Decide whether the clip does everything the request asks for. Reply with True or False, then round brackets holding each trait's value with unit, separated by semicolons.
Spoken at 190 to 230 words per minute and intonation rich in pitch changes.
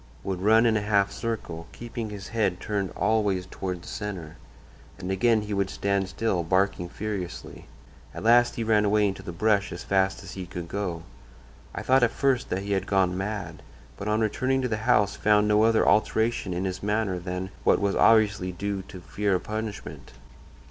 False (195 wpm; 2.5 semitones)